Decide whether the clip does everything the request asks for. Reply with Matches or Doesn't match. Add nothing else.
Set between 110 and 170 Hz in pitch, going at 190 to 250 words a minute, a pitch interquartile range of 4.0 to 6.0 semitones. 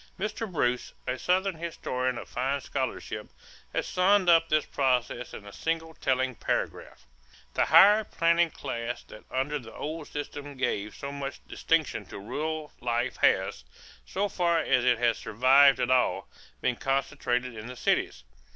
Doesn't match